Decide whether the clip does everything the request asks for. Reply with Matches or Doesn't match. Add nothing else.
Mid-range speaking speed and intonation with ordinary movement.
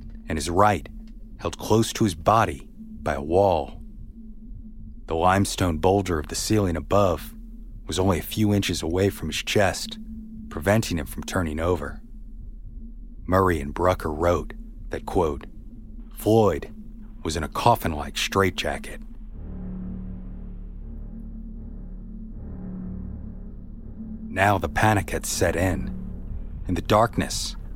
Doesn't match